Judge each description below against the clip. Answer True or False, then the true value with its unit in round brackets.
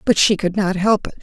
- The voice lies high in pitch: True (195 Hz)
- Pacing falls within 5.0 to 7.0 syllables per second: True (5.7 syllables/s)